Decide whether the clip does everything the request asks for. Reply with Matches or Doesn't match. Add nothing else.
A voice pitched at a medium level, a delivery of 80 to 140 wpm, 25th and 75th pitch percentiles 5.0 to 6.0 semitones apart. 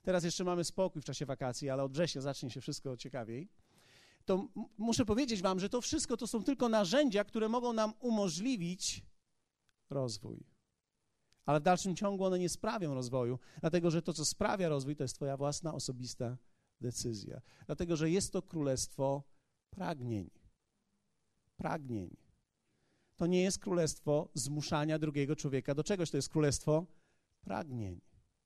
Doesn't match